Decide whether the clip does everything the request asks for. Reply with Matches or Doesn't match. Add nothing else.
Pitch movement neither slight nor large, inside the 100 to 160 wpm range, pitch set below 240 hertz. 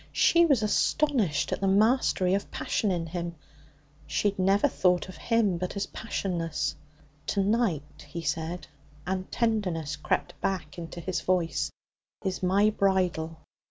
Matches